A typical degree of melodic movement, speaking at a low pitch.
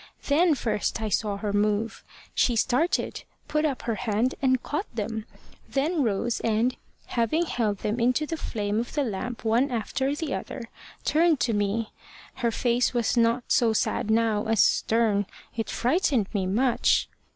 No: average, 3.4 semitones; high, 230 Hz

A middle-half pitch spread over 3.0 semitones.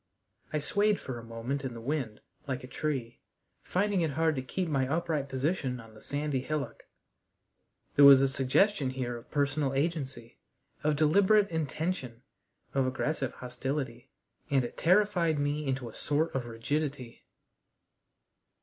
Yes: average, 3.5 semitones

